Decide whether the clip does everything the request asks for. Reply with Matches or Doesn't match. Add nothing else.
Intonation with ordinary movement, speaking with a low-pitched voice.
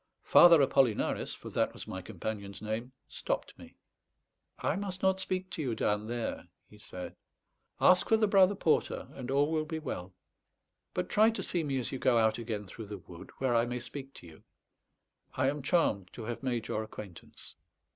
Doesn't match